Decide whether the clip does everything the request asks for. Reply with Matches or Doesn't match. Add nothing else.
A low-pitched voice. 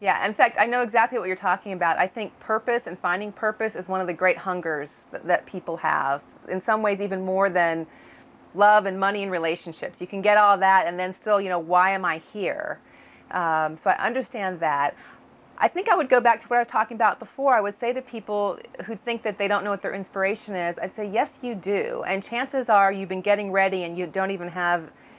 Doesn't match